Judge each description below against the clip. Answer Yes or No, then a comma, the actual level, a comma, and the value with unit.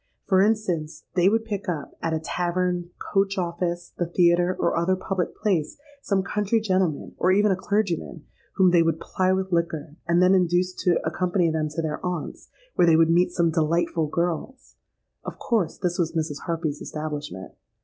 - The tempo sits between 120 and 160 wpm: No, average, 180 wpm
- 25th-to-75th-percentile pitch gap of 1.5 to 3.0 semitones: Yes, narrow, 2.4 semitones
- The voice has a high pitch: No, medium, 175 Hz